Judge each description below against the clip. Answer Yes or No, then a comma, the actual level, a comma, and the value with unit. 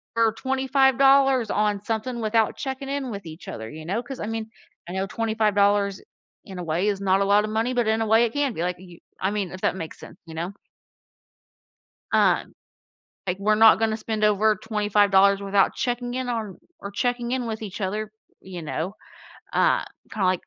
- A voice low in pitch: No, high, 215 Hz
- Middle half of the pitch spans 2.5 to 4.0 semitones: Yes, average, 3.1 semitones